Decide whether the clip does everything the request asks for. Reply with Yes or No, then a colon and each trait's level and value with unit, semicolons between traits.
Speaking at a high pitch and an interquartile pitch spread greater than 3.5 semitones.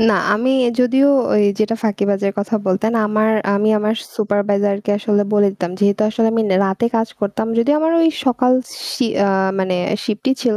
No: high, 210 Hz; narrow, 2.4 semitones